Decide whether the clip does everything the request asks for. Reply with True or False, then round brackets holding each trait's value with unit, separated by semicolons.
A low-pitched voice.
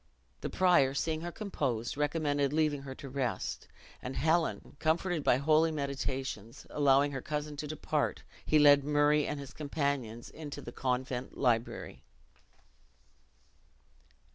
False (145 Hz)